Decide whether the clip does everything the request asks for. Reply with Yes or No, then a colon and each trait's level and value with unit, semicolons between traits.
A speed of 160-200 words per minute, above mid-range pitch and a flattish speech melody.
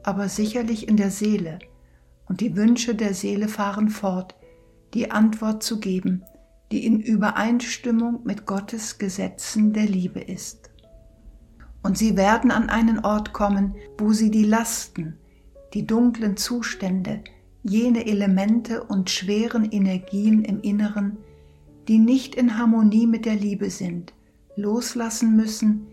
No: average, 130 wpm; high, 215 Hz; narrow, 2.3 semitones